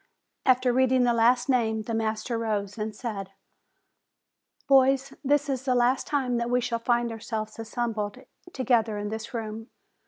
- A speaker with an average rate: Yes, average, 165 wpm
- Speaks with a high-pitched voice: Yes, high, 235 Hz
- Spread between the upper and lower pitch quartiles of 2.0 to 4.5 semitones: Yes, narrow, 2.5 semitones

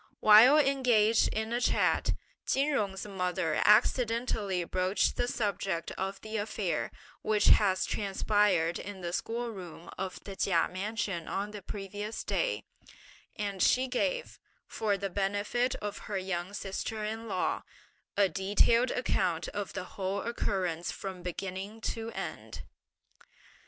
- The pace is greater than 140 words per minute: No, slow, 135 wpm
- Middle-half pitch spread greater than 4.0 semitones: No, average, 2.9 semitones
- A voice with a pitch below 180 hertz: No, high, 205 Hz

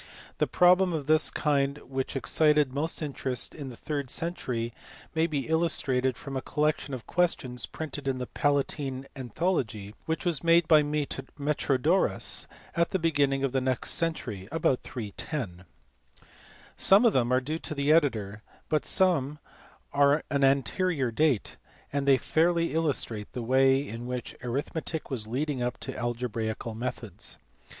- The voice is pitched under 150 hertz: Yes, medium, 140 Hz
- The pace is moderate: Yes, average, 155 wpm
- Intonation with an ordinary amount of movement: Yes, average, 3.8 semitones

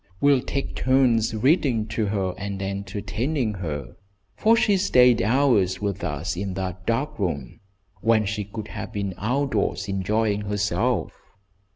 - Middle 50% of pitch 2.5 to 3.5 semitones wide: No, average, 4.3 semitones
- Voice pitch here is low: Yes, low, 105 Hz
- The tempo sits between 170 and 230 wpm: No, average, 140 wpm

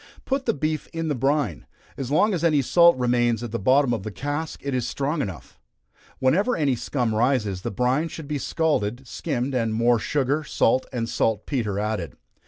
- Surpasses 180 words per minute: Yes, average, 190 wpm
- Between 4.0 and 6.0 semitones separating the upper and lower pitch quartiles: Yes, average, 4.7 semitones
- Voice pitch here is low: Yes, low, 130 Hz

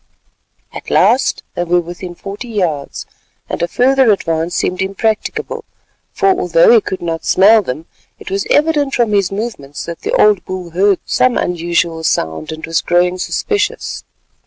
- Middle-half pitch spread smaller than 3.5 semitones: No, wide, 5.6 semitones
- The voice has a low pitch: No, high, 190 Hz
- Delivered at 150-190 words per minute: Yes, average, 160 wpm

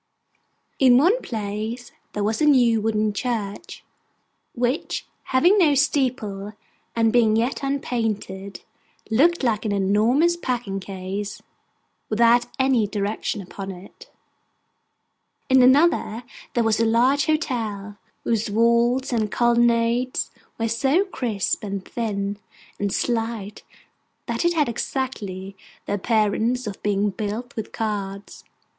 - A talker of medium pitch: No, high, 230 Hz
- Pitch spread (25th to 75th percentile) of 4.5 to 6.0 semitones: No, average, 3.6 semitones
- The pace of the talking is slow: Yes, slow, 120 wpm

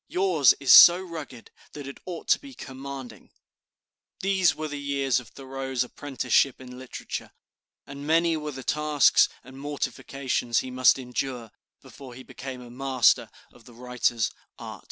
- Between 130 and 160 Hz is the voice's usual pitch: Yes, low, 135 Hz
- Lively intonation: No, average, 2.7 semitones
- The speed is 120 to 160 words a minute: Yes, average, 155 wpm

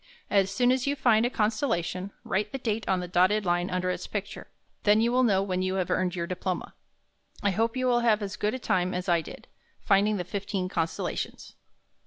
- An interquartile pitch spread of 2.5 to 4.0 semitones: Yes, average, 3.6 semitones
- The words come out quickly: Yes, fast, 220 wpm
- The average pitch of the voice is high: Yes, high, 195 Hz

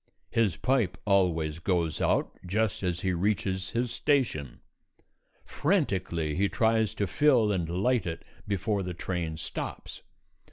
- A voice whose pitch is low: Yes, very low, 95 Hz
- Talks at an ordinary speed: No, slow, 130 wpm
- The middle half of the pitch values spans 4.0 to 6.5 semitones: Yes, average, 4.5 semitones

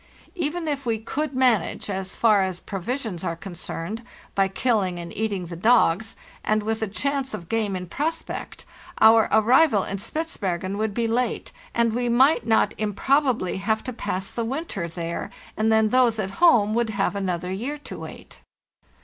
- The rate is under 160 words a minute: No, average, 170 wpm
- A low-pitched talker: No, high, 220 Hz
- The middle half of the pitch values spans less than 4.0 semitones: No, average, 4.4 semitones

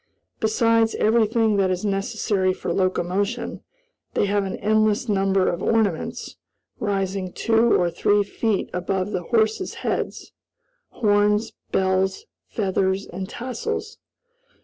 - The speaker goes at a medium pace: No, slow, 115 wpm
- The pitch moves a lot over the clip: No, average, 2.8 semitones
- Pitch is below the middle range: No, high, 205 Hz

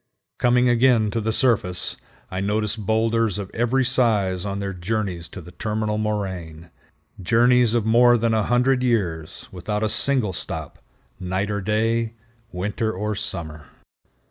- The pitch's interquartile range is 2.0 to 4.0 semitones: Yes, average, 3.5 semitones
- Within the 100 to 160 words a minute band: Yes, average, 145 wpm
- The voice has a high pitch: No, low, 110 Hz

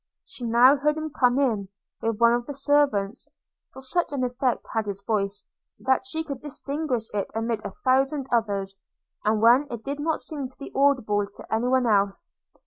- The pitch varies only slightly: No, average, 4.3 semitones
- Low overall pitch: No, very high, 250 Hz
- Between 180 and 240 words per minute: Yes, average, 190 wpm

